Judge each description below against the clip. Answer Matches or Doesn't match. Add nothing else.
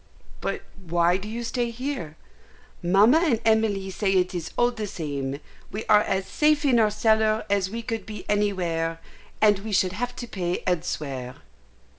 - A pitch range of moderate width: Matches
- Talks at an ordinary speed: Matches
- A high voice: Matches